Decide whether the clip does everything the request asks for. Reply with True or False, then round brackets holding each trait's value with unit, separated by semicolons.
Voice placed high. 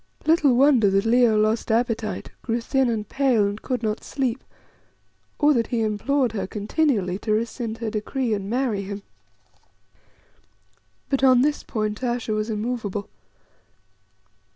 True (230 Hz)